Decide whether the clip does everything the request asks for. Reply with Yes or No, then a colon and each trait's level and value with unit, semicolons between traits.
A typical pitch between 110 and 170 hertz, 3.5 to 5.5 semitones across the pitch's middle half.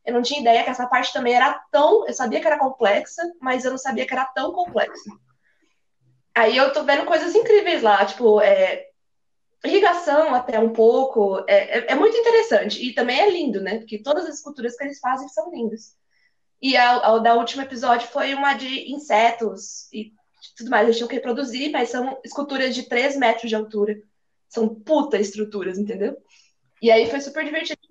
No: very high, 255 Hz; average, 4.4 semitones